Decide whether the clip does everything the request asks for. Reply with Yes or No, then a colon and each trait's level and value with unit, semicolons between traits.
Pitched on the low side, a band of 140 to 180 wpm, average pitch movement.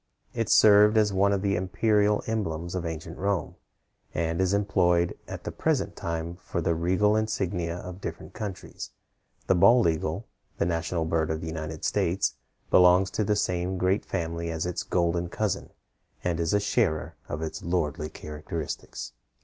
Yes: very low, 90 Hz; average, 165 wpm; average, 3.3 semitones